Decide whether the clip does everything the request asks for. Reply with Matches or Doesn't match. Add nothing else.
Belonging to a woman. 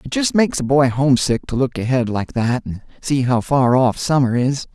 Doesn't match